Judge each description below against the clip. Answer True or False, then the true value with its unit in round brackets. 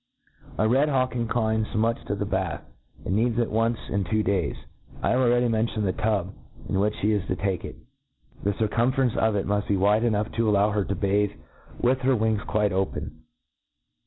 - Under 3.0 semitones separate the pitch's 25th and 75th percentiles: True (2.5 semitones)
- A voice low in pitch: True (110 Hz)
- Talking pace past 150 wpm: True (200 wpm)